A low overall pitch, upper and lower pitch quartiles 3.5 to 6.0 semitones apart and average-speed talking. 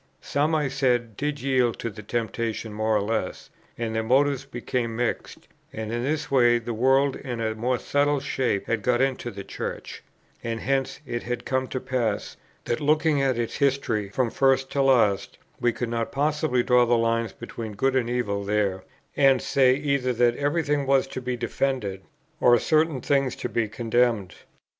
No: low, 125 Hz; average, 3.0 semitones; average, 185 wpm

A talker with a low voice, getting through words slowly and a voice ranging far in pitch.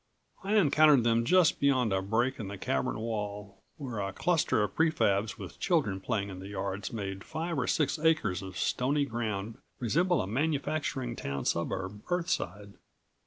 No: low, 115 Hz; average, 165 wpm; wide, 7.0 semitones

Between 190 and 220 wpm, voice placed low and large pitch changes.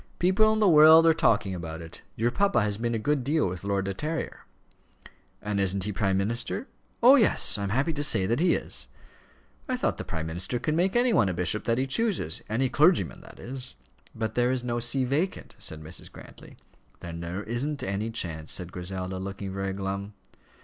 Yes: fast, 205 wpm; low, 110 Hz; wide, 7.5 semitones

